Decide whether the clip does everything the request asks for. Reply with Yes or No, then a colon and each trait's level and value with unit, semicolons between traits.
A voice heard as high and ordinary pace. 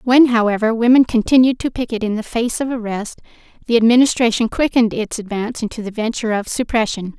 Yes: high, 230 Hz; average, 175 wpm